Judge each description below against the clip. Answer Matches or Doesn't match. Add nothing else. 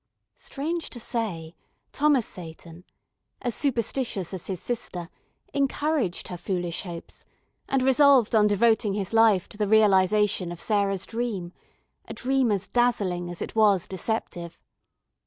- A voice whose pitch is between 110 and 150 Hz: Doesn't match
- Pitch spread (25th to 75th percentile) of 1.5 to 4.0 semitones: Doesn't match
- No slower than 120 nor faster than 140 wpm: Matches